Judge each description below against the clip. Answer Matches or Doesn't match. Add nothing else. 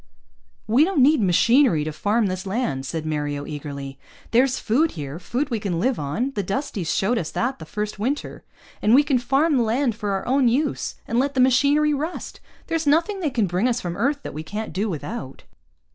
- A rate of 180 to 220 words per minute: Matches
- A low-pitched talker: Doesn't match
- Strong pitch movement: Matches